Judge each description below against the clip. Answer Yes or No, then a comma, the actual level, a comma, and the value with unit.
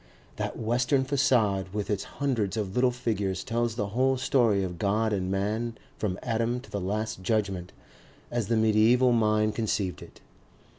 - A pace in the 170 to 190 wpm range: No, average, 160 wpm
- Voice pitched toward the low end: Yes, low, 110 Hz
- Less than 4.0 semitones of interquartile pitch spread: Yes, average, 3.2 semitones